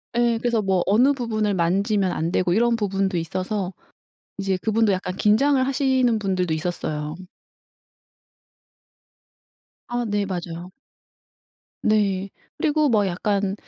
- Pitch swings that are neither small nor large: Yes, average, 3.9 semitones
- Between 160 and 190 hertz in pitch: No, high, 200 Hz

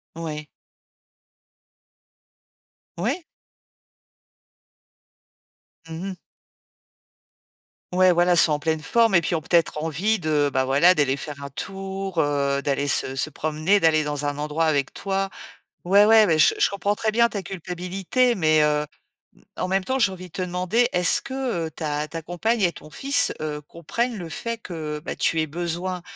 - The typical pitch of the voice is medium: Yes, medium, 170 Hz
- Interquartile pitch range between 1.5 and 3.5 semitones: No, average, 4.2 semitones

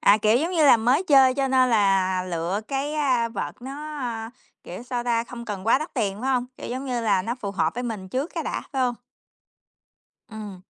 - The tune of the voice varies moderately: Yes, average, 4.3 semitones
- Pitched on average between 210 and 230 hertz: No, high, 240 Hz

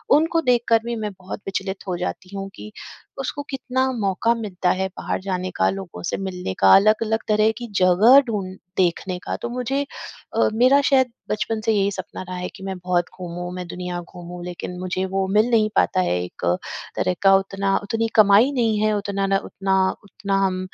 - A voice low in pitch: No, high, 195 Hz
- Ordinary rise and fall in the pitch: Yes, average, 3.5 semitones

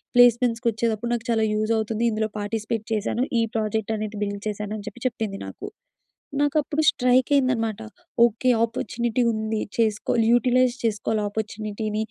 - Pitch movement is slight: Yes, narrow, 1.9 semitones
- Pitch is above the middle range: Yes, high, 225 Hz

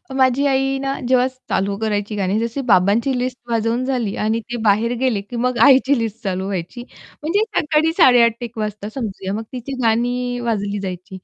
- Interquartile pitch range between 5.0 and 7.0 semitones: No, average, 3.8 semitones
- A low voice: No, high, 230 Hz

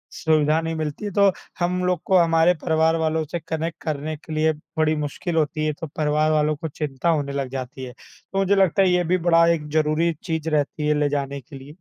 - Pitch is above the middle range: No, medium, 155 Hz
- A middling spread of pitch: No, narrow, 2.0 semitones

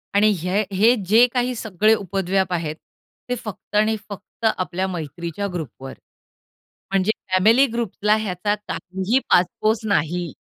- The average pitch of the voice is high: Yes, high, 195 Hz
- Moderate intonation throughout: Yes, average, 3.4 semitones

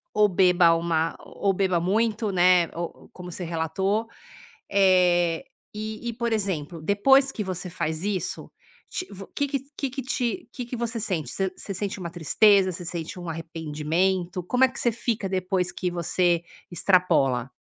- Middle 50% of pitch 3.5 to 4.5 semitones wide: Yes, average, 3.8 semitones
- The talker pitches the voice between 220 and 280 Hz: No, medium, 185 Hz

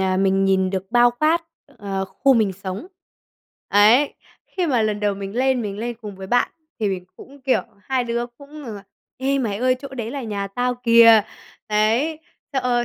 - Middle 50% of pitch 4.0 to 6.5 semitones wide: Yes, average, 4.4 semitones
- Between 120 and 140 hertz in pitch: No, high, 230 Hz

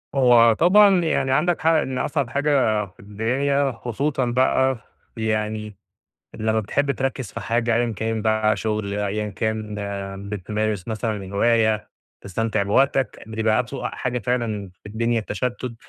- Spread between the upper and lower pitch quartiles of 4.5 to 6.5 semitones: No, average, 3.5 semitones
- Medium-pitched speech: No, low, 115 Hz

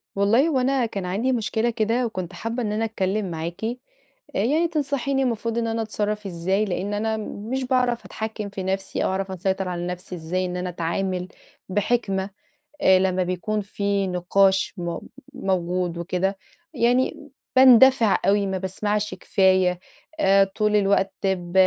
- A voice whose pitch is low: No, high, 200 Hz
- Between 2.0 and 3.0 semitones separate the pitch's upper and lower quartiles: No, average, 3.4 semitones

